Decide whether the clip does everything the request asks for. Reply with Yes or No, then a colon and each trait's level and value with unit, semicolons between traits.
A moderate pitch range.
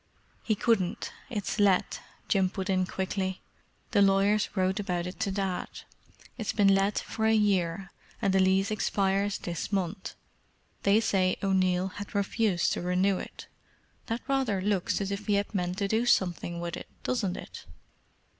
No: narrow, 1.9 semitones